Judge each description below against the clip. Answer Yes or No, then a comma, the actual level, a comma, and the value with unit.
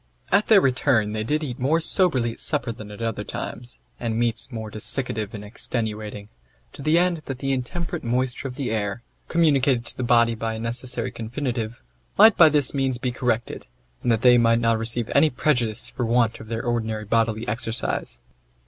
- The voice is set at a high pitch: No, low, 120 Hz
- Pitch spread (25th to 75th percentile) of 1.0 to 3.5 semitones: Yes, average, 3.1 semitones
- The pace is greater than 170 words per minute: Yes, average, 190 wpm